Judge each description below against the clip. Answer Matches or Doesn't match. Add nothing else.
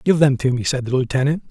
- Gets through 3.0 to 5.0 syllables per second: Doesn't match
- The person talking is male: Matches